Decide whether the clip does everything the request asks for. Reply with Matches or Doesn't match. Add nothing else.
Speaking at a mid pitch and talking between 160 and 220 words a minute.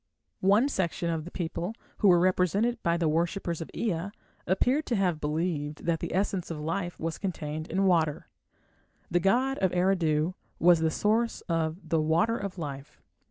Matches